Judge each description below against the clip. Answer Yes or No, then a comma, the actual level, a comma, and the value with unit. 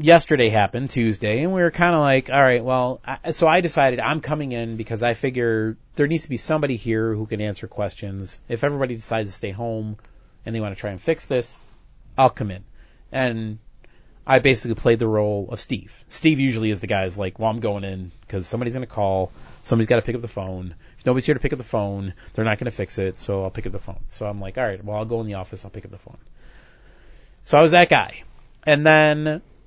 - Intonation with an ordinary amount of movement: Yes, average, 4.3 semitones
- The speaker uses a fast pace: Yes, fast, 250 wpm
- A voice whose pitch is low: Yes, low, 115 Hz